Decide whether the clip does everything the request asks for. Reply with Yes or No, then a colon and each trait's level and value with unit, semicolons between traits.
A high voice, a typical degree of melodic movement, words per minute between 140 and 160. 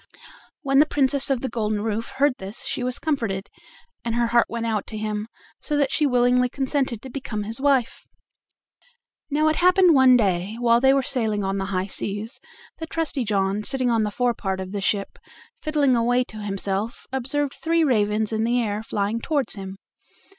No: high, 235 Hz; average, 4.4 semitones; average, 190 wpm